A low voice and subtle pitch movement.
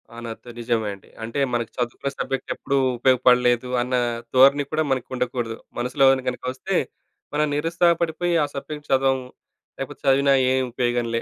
Yes: low, 130 Hz; narrow, 2.3 semitones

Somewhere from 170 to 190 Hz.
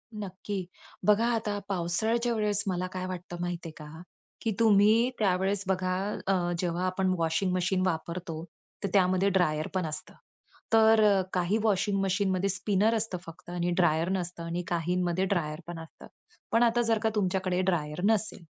Yes: medium, 185 Hz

